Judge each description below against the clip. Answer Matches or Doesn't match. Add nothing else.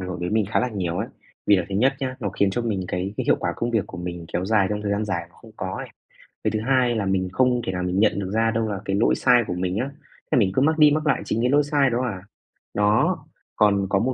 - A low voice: Matches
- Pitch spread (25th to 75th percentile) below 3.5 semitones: Doesn't match